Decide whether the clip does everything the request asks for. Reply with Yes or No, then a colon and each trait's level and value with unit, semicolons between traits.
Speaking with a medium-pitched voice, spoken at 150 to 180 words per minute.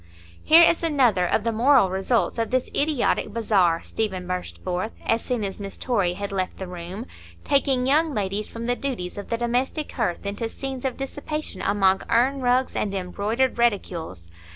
No: high, 225 Hz; average, 175 wpm